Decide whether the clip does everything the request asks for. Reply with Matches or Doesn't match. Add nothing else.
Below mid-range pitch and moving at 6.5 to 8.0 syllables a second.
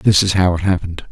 Matches